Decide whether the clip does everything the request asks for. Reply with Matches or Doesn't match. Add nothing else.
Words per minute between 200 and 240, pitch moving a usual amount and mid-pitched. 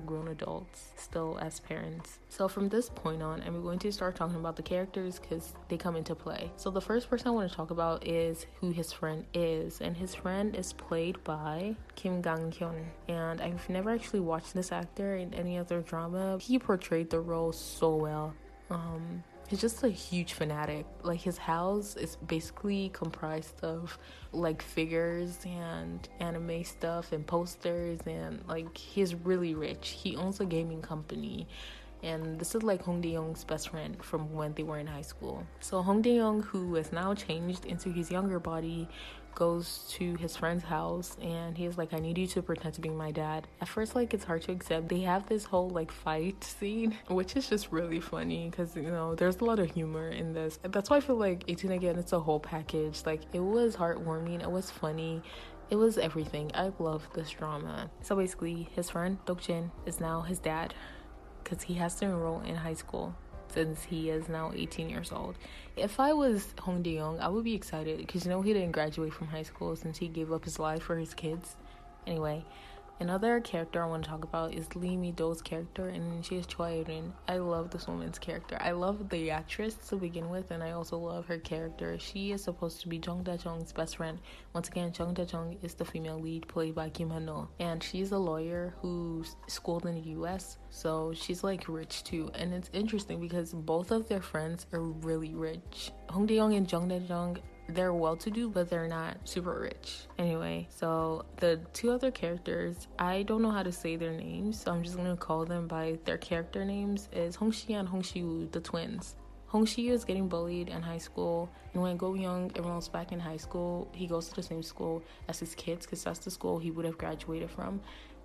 Doesn't match